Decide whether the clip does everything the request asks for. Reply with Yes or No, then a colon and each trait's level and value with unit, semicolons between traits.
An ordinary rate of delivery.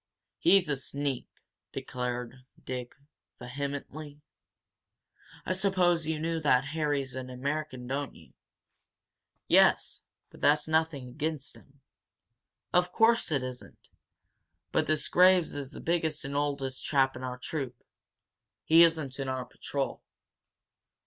No: slow, 120 wpm